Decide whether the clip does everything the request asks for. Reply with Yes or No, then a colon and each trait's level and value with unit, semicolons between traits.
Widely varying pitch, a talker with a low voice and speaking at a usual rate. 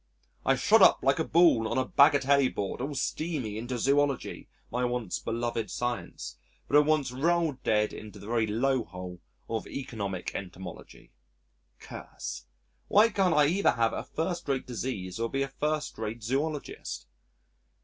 No: average, 4.8 semitones; low, 125 Hz; average, 160 wpm